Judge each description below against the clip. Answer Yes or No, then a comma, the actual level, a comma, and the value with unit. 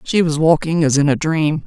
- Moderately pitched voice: Yes, medium, 155 Hz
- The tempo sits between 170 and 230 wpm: No, fast, 255 wpm